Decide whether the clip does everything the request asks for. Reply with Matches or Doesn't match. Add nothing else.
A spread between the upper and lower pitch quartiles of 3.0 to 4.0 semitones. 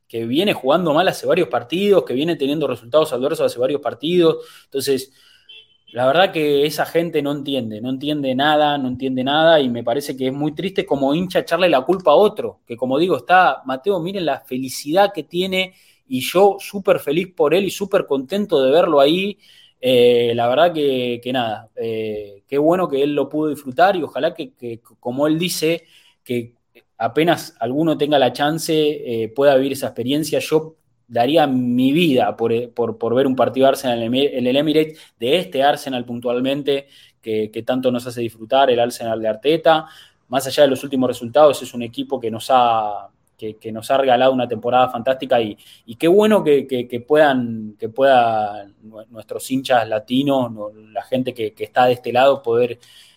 Doesn't match